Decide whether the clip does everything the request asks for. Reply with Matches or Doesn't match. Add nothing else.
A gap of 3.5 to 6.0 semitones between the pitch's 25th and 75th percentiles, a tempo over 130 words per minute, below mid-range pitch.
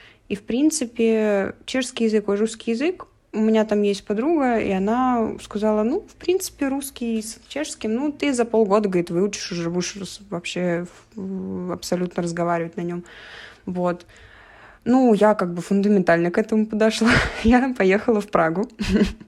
Doesn't match